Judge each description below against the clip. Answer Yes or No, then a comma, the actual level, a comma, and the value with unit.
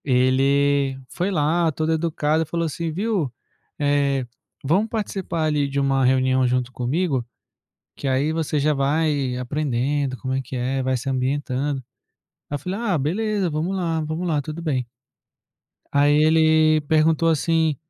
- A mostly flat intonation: No, average, 3.3 semitones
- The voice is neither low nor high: Yes, medium, 145 Hz